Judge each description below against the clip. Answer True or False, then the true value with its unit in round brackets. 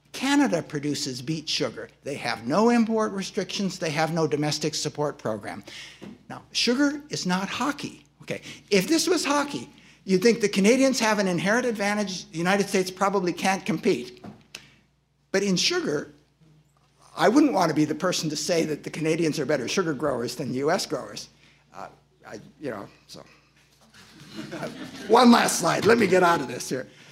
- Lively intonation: True (6.0 semitones)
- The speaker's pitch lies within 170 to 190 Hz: True (185 Hz)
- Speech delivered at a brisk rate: False (170 wpm)